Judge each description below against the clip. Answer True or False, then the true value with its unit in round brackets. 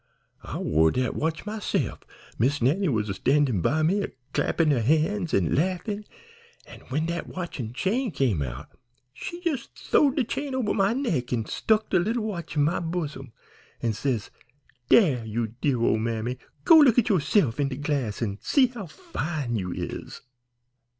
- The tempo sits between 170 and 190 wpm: True (175 wpm)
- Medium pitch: True (150 Hz)